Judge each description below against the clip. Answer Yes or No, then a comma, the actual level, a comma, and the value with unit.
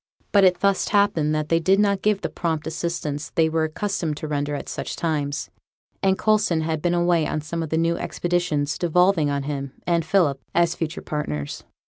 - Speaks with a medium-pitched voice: Yes, medium, 165 Hz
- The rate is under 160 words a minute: No, average, 195 wpm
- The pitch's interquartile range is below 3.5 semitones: Yes, average, 2.9 semitones